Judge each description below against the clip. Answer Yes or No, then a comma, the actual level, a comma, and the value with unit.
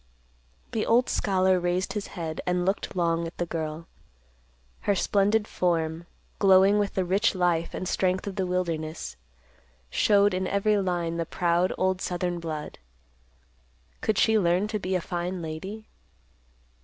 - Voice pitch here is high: No, medium, 180 Hz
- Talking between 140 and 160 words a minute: Yes, average, 150 wpm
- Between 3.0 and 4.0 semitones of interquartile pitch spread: No, narrow, 2.6 semitones